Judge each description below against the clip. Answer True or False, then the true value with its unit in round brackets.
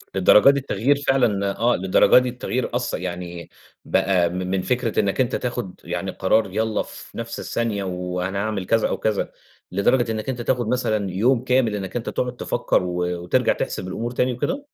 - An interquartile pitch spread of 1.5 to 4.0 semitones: False (4.7 semitones)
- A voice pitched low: True (110 Hz)